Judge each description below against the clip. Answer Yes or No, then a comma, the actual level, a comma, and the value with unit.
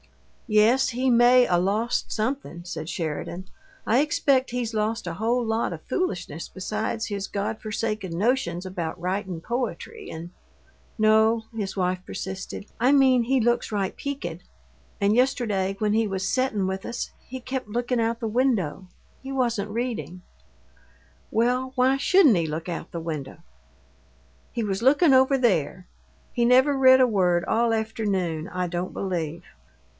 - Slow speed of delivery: No, average, 155 wpm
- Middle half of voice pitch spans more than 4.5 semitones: Yes, average, 5.2 semitones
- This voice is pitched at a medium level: No, high, 220 Hz